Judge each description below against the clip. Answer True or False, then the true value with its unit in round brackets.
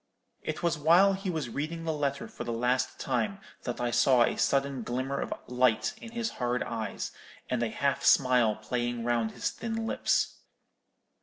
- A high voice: False (130 Hz)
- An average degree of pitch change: True (4.9 semitones)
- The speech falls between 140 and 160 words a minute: False (175 wpm)